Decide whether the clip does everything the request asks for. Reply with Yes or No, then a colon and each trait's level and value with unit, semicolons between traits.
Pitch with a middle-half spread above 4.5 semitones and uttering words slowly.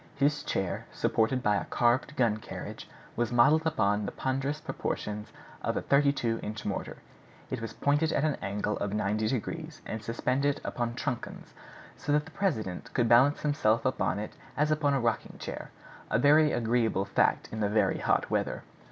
No: average, 5.1 semitones; average, 175 wpm